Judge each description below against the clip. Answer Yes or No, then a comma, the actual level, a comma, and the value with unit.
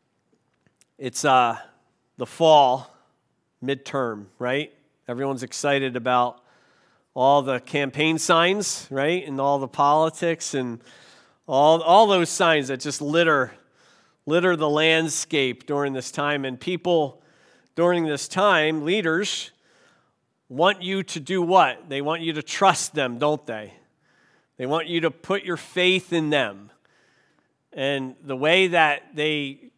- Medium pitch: Yes, medium, 150 Hz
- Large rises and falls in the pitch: No, average, 3.8 semitones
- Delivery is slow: Yes, slow, 130 wpm